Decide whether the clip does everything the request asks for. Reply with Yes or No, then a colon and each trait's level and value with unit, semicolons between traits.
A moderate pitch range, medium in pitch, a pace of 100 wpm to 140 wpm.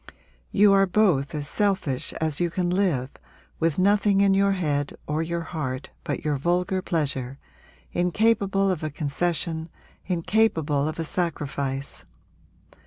Yes: average, 4.7 semitones; medium, 170 Hz; slow, 135 wpm